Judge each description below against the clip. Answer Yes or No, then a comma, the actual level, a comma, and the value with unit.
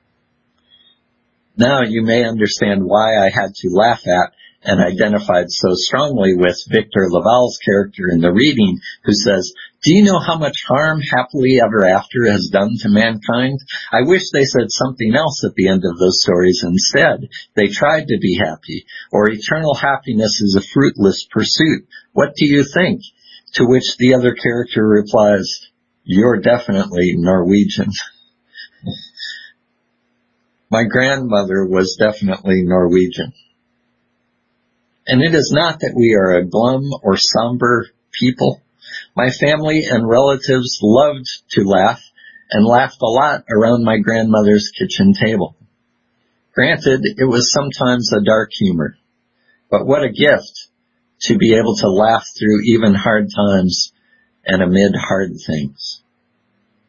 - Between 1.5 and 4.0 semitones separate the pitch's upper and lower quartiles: No, average, 4.8 semitones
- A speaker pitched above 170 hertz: No, low, 115 Hz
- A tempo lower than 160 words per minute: Yes, average, 140 wpm